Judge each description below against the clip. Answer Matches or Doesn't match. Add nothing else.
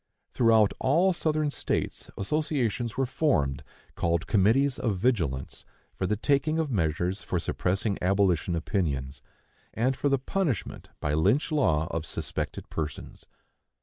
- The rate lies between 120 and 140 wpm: Matches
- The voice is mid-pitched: Doesn't match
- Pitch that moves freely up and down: Matches